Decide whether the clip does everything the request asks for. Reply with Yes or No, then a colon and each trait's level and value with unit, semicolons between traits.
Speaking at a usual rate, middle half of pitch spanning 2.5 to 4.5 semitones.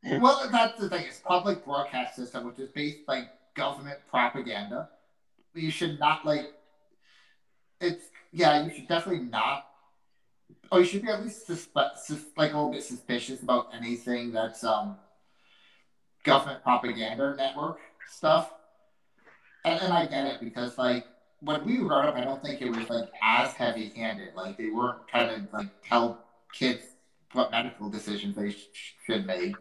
No: average, 165 wpm; average, 5.0 semitones